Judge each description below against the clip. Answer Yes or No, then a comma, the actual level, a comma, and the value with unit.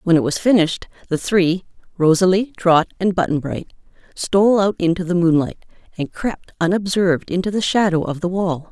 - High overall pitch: No, medium, 180 Hz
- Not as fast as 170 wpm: Yes, average, 160 wpm